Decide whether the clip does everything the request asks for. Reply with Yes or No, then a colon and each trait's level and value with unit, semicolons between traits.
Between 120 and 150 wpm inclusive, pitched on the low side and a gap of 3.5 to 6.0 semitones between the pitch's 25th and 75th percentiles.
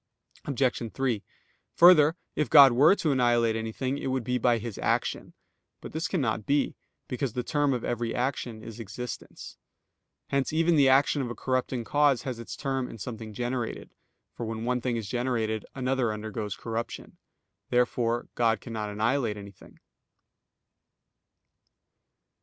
No: average, 145 wpm; low, 125 Hz; average, 2.9 semitones